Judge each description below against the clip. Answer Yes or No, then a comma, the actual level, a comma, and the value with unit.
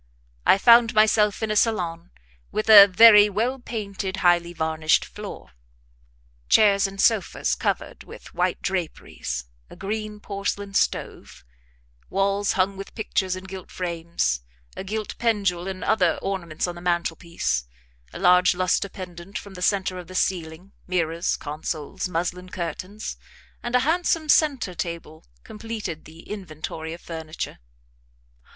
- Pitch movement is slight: No, average, 3.6 semitones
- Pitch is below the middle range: No, medium, 185 Hz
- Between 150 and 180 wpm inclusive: No, slow, 135 wpm